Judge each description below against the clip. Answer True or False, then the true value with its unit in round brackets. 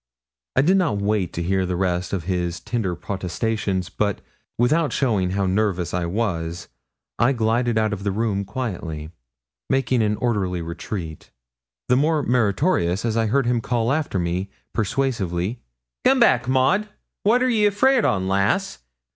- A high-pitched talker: False (105 Hz)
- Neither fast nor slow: True (155 wpm)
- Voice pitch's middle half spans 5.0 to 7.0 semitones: True (5.6 semitones)